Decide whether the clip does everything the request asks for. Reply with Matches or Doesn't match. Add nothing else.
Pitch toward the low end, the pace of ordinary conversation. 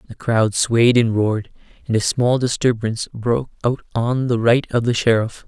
Matches